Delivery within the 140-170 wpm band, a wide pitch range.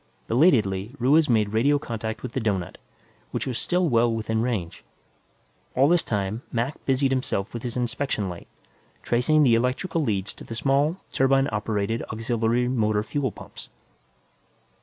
No: average, 150 wpm; average, 3.6 semitones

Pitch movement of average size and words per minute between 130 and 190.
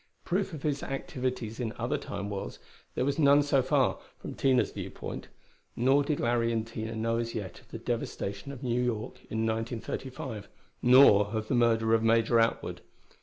Yes: average, 3.3 semitones; average, 175 wpm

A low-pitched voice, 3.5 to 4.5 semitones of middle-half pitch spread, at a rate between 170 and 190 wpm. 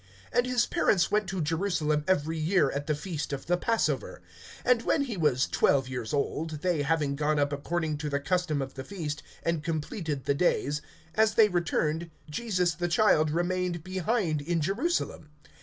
No: medium, 165 Hz; average, 3.9 semitones; average, 175 wpm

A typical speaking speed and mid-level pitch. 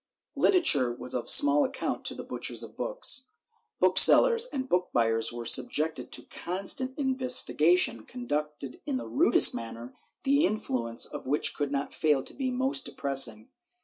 Yes: average, 155 wpm; medium, 160 Hz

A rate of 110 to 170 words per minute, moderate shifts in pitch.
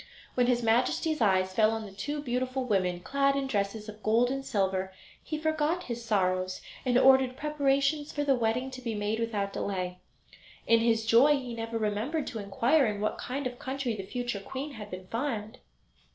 No: average, 190 wpm; average, 4.5 semitones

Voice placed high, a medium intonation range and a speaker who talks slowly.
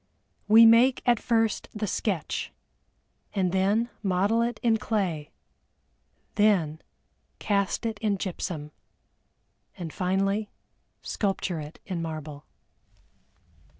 Yes: high, 195 Hz; average, 4.1 semitones; slow, 95 wpm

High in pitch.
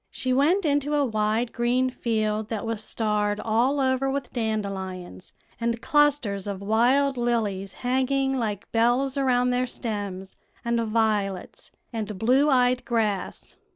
Yes: high, 235 Hz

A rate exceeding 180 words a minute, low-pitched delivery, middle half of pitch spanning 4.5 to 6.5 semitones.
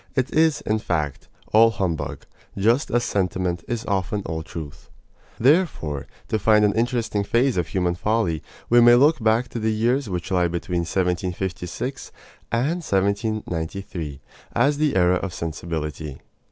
No: average, 145 wpm; low, 100 Hz; average, 5.2 semitones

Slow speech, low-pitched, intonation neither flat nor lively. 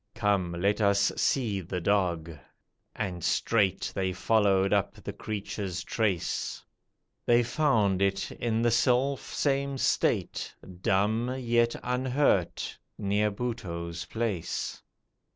Yes: slow, 105 wpm; low, 105 Hz; average, 3.7 semitones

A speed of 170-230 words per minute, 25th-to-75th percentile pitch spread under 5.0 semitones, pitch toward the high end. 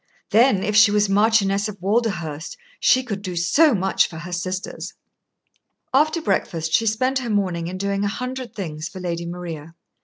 Yes: average, 175 wpm; average, 4.3 semitones; high, 195 Hz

